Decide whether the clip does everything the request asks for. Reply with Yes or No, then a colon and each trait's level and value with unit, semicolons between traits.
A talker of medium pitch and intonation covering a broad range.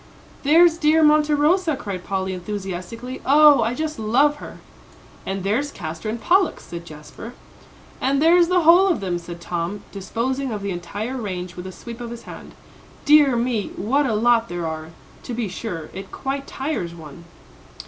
No: high, 230 Hz; wide, 7.7 semitones